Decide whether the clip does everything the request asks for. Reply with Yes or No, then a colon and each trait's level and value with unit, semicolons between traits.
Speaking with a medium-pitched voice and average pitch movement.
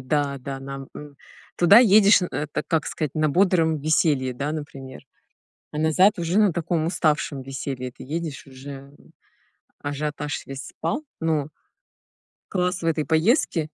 Yes: medium, 155 Hz; average, 3.6 semitones